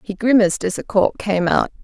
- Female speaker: Yes, female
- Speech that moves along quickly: Yes, fast, 230 wpm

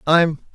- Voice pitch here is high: No, medium, 160 Hz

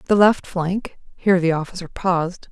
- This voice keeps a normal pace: Yes, average, 165 wpm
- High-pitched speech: No, medium, 180 Hz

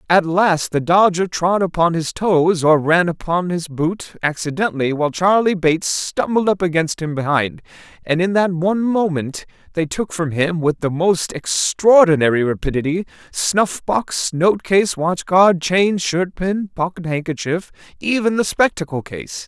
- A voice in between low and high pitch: Yes, medium, 175 Hz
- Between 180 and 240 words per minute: No, average, 155 wpm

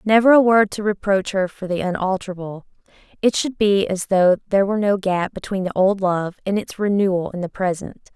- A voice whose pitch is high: Yes, high, 195 Hz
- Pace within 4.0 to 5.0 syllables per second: No, 5.6 syllables/s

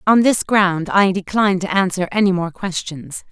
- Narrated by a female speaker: Yes, female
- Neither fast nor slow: Yes, average, 180 wpm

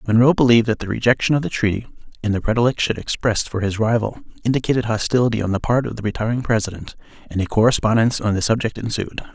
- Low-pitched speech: Yes, low, 115 Hz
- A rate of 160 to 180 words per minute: No, average, 200 wpm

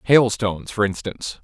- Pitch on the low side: Yes, low, 110 Hz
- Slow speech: Yes, slow, 125 wpm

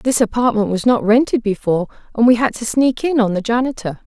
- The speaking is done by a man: No, female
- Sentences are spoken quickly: Yes, fast, 215 wpm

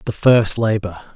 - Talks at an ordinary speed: Yes, average, 155 wpm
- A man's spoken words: Yes, male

